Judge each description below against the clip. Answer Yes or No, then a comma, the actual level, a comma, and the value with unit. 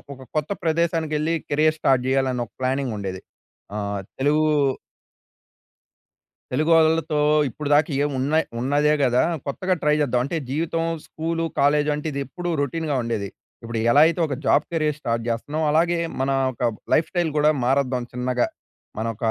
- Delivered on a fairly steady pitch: No, average, 3.8 semitones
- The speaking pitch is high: No, medium, 145 Hz